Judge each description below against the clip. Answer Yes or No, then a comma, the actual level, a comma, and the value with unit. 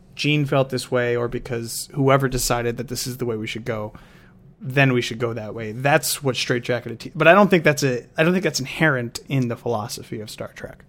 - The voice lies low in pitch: Yes, low, 125 Hz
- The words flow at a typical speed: No, fast, 240 wpm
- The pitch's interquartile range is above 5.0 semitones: No, average, 3.5 semitones